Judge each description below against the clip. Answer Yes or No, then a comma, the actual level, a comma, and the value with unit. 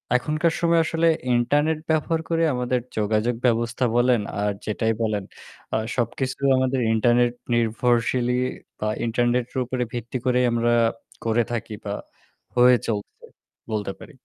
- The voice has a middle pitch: No, low, 120 Hz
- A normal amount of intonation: No, narrow, 2.0 semitones